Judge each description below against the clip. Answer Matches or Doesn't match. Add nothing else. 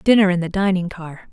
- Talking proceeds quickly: Matches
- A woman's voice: Matches